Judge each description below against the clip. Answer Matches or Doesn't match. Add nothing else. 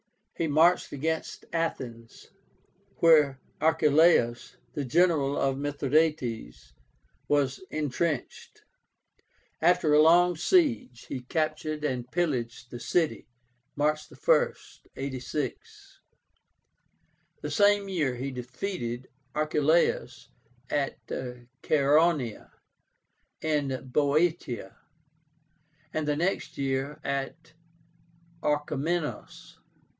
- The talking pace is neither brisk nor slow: Doesn't match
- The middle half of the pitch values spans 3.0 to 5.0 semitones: Matches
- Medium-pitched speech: Matches